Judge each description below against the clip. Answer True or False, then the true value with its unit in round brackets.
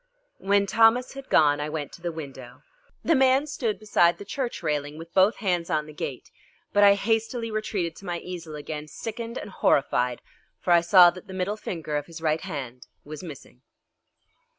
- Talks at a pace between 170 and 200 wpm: True (190 wpm)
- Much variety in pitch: True (5.9 semitones)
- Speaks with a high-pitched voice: False (175 Hz)